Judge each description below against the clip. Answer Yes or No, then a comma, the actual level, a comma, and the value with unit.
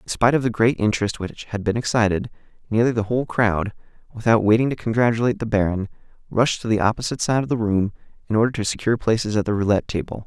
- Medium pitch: No, low, 110 Hz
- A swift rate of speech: Yes, fast, 215 wpm